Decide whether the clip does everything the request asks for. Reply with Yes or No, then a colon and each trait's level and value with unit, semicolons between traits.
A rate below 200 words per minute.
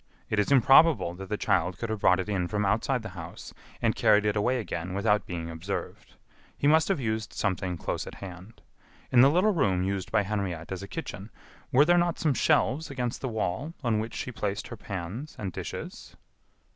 No: fast, 205 wpm